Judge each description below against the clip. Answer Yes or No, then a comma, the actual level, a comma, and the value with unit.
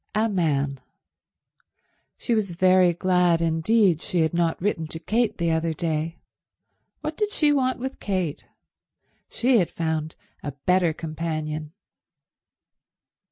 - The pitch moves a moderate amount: Yes, average, 4.4 semitones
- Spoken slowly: Yes, slow, 125 wpm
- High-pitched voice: No, medium, 170 Hz